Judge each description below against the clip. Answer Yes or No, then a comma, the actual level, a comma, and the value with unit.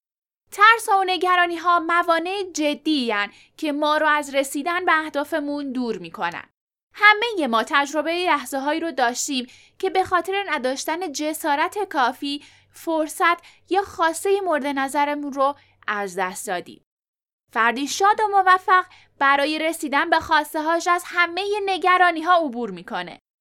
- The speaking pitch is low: No, very high, 315 Hz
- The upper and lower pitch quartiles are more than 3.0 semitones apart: Yes, average, 4.2 semitones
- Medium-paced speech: Yes, average, 135 wpm